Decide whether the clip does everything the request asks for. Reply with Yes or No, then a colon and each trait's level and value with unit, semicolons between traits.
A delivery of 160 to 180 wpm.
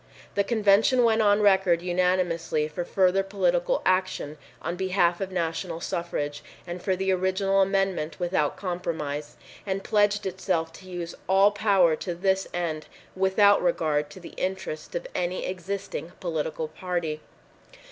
No: average, 140 wpm